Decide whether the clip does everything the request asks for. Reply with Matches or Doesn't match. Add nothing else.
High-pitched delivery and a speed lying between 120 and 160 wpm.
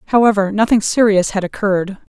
Matches